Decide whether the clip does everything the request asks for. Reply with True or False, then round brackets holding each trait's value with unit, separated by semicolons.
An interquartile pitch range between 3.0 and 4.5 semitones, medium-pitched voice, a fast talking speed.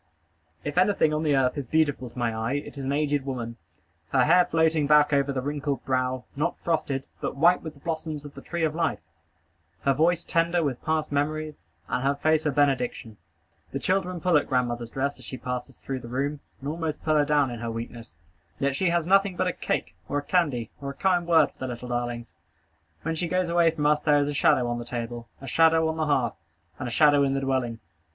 True (3.7 semitones; 145 Hz; 230 wpm)